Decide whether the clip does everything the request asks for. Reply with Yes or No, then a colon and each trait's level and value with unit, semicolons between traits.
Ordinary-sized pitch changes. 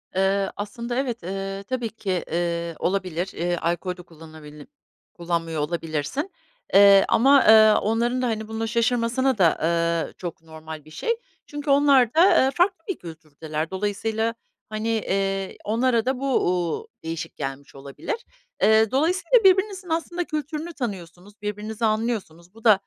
No: wide, 6.6 semitones